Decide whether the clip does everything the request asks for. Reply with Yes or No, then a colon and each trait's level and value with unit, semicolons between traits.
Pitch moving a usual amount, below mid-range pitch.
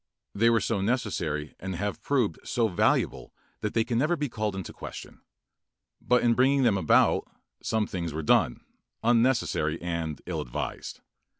No: wide, 5.9 semitones; low, 105 Hz